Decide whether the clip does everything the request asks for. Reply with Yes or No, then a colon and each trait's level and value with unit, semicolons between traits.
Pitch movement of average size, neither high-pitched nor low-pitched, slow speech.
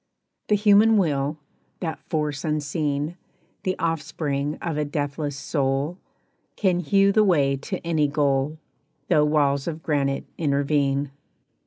Yes: average, 3.0 semitones; medium, 150 Hz; slow, 125 wpm